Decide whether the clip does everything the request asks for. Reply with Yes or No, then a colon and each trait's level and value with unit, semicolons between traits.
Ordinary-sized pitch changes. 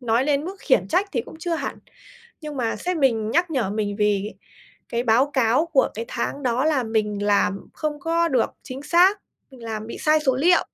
No: wide, 5.8 semitones